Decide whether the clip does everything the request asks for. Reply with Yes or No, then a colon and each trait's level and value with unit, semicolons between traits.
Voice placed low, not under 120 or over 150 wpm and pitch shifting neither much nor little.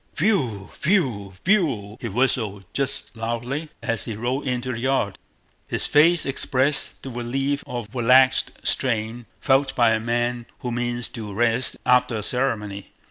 Yes: low, 120 Hz; average, 145 wpm; average, 3.0 semitones